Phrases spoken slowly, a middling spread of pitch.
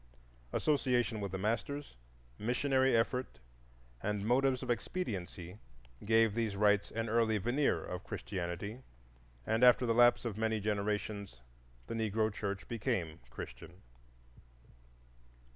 Yes: slow, 115 wpm; average, 3.0 semitones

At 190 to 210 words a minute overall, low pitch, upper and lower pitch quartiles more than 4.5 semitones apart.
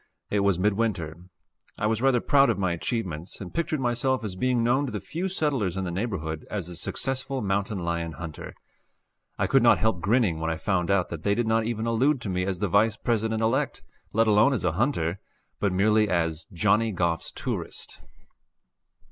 Yes: average, 195 wpm; low, 105 Hz; average, 4.9 semitones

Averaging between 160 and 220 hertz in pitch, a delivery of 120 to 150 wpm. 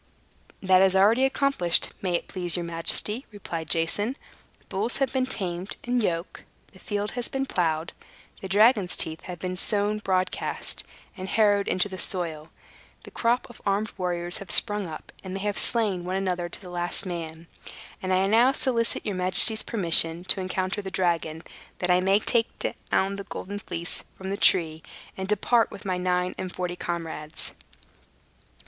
No: high, 190 Hz; average, 175 wpm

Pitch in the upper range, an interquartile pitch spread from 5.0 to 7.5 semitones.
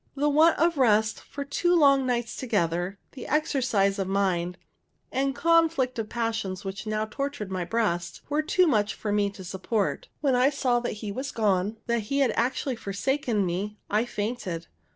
Yes: high, 225 Hz; wide, 5.4 semitones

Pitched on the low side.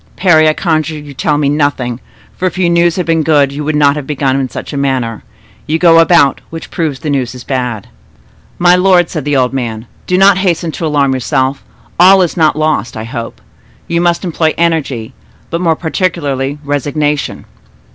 No: medium, 150 Hz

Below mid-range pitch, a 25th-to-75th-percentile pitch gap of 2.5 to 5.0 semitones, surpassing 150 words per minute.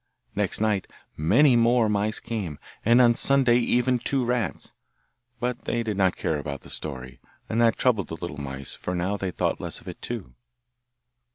No: low, 110 Hz; wide, 5.6 semitones; average, 180 wpm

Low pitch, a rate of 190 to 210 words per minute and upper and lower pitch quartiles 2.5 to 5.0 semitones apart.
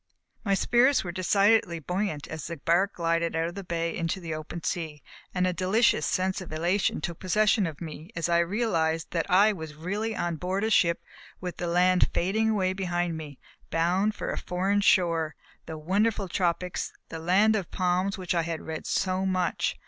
No: medium, 180 Hz; average, 195 wpm; average, 2.8 semitones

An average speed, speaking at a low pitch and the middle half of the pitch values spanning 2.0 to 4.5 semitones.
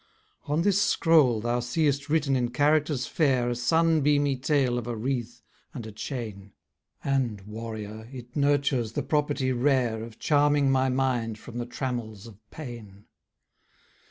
Yes: average, 150 wpm; low, 125 Hz; average, 3.7 semitones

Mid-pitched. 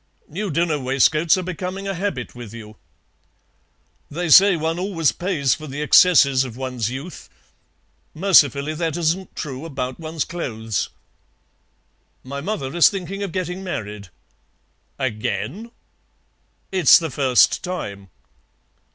Yes: medium, 155 Hz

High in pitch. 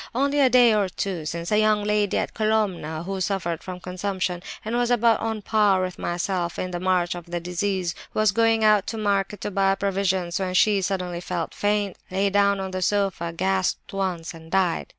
Yes: high, 195 Hz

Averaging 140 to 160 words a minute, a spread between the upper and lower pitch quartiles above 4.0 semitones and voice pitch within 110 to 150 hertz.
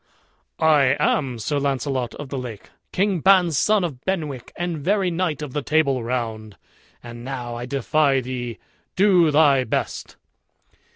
Yes: average, 150 wpm; average, 4.8 semitones; medium, 140 Hz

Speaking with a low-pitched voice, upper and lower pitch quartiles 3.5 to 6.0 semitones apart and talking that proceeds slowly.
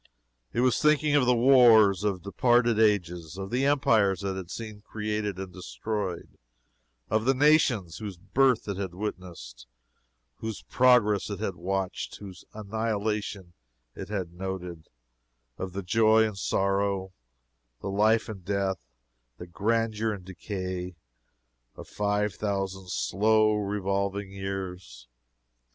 No: low, 100 Hz; average, 2.7 semitones; slow, 130 wpm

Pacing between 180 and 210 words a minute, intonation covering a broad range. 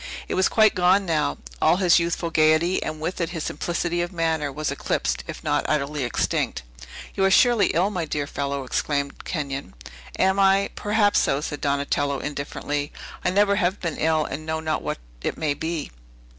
No: average, 185 wpm; average, 3.9 semitones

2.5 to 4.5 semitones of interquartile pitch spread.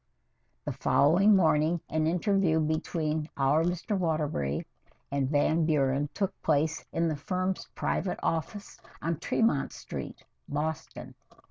Yes: average, 3.1 semitones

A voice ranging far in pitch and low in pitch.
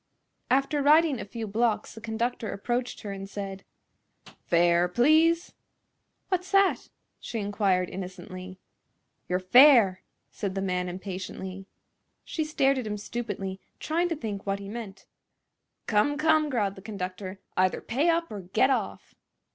No: wide, 6.1 semitones; high, 210 Hz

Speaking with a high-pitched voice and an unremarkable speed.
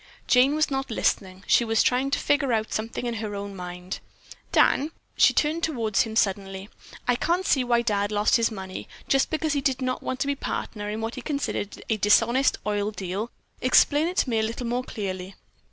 No: high, 230 Hz; fast, 210 wpm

